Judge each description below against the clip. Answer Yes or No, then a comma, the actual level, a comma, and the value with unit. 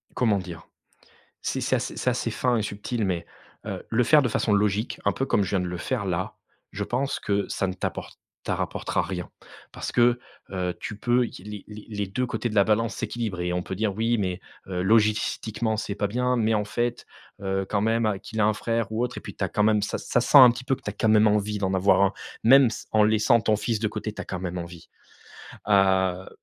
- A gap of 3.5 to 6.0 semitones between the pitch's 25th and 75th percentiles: No, average, 3.0 semitones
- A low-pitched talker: Yes, low, 105 Hz